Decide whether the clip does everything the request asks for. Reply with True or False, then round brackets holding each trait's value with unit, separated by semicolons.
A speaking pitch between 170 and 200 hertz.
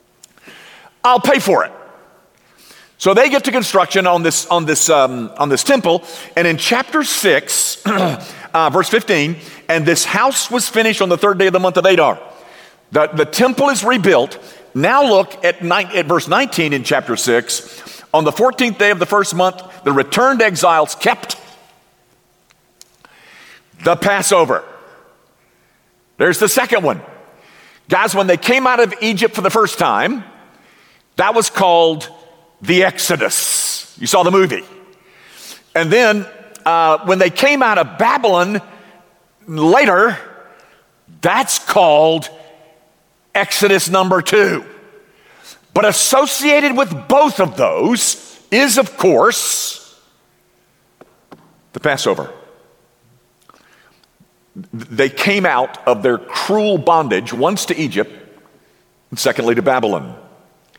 True (190 Hz)